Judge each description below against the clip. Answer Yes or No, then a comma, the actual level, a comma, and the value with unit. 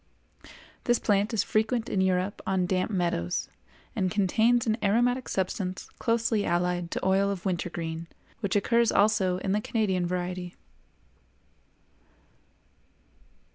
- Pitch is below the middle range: No, high, 190 Hz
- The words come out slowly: Yes, slow, 120 wpm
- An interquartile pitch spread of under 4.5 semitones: Yes, average, 3.4 semitones